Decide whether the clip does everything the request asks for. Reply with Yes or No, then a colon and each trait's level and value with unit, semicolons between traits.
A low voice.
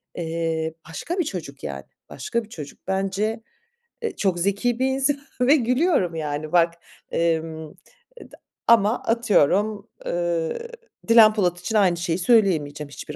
No: high, 190 Hz